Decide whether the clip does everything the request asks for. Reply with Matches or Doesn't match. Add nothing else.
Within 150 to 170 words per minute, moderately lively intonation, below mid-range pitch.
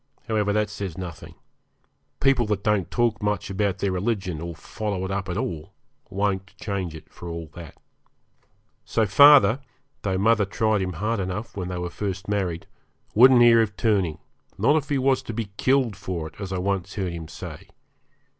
Doesn't match